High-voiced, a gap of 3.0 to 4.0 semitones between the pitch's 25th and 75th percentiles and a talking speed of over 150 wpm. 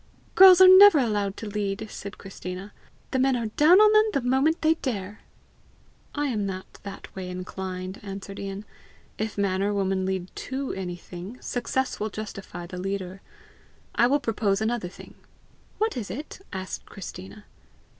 No: high, 205 Hz; wide, 5.5 semitones; average, 160 wpm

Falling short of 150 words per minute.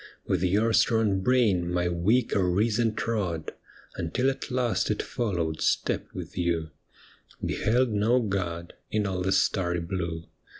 Yes: average, 140 wpm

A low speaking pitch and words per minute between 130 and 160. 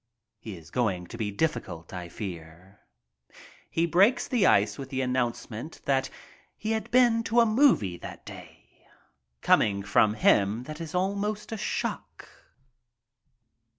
Yes: low, 125 Hz; average, 140 wpm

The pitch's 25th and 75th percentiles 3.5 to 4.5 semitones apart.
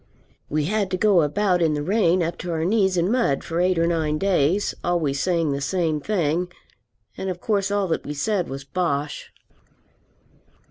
Yes: average, 4.0 semitones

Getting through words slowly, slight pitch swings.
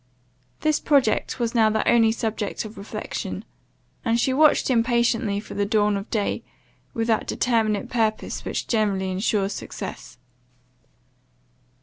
Yes: slow, 130 wpm; narrow, 2.3 semitones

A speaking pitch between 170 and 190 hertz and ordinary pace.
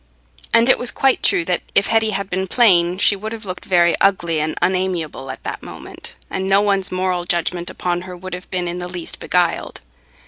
No: medium, 185 Hz; fast, 210 wpm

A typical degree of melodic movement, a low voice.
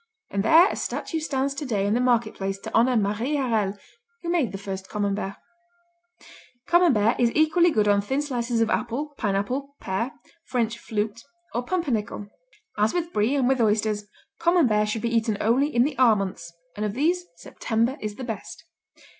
No: average, 4.8 semitones; high, 230 Hz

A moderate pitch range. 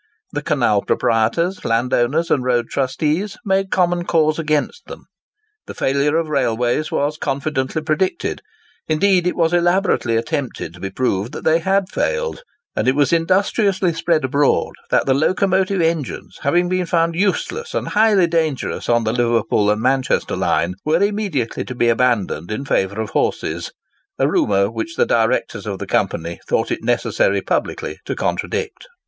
No: wide, 6.7 semitones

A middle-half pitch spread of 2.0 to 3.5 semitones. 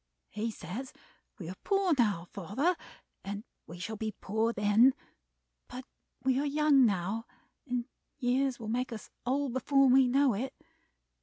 No: average, 4.3 semitones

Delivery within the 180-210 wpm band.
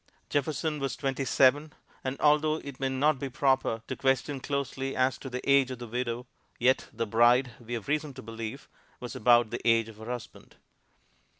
Yes: average, 190 wpm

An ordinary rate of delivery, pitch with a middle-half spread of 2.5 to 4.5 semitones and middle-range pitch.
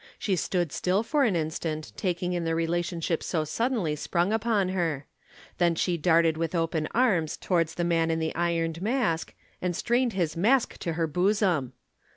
Yes: average, 175 wpm; average, 2.8 semitones; medium, 170 Hz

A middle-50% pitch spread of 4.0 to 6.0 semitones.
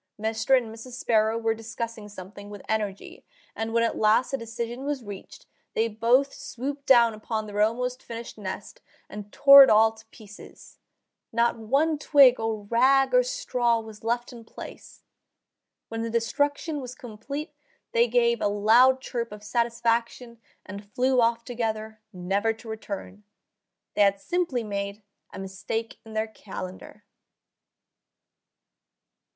No: average, 2.8 semitones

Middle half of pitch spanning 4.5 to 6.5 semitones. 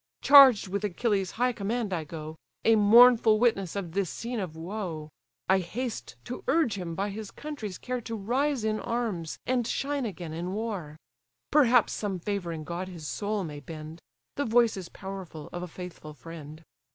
Yes: wide, 5.5 semitones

